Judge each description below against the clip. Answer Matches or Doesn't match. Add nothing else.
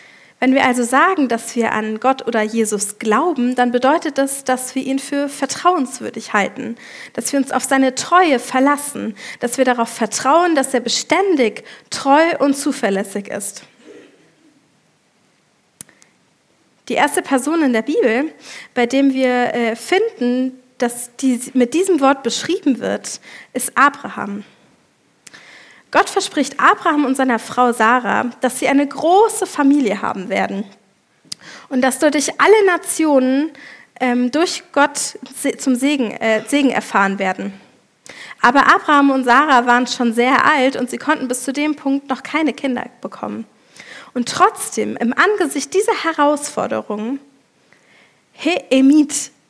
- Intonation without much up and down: Doesn't match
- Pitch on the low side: Doesn't match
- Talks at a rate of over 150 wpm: Doesn't match